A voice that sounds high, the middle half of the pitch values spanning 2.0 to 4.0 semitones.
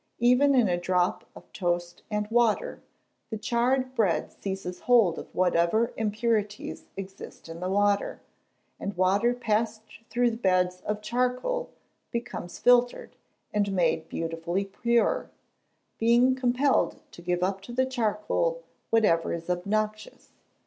No: high, 210 Hz; average, 4.7 semitones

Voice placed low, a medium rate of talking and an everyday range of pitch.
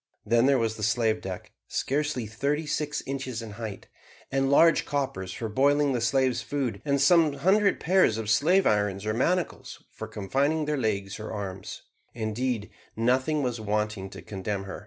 Yes: low, 120 Hz; average, 170 wpm; average, 5.0 semitones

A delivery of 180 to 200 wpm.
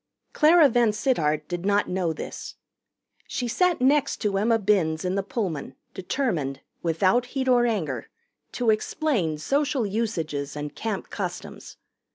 No: slow, 135 wpm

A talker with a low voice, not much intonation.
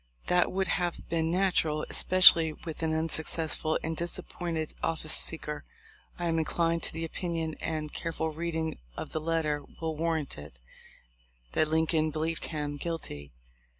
No: medium, 160 Hz; narrow, 1.2 semitones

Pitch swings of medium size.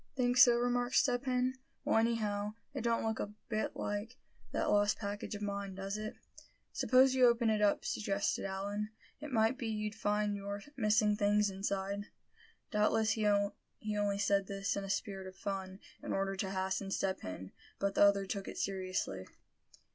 No: narrow, 2.0 semitones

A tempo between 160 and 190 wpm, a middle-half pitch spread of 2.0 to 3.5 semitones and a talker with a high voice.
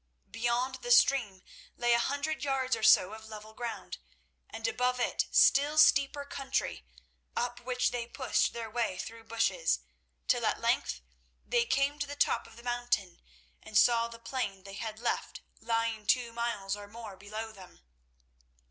Yes: average, 165 wpm; narrow, 2.6 semitones; high, 235 Hz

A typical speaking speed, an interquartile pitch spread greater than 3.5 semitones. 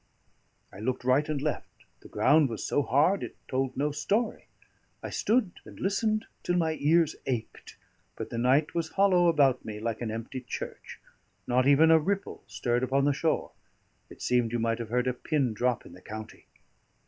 Yes: average, 185 wpm; average, 4.9 semitones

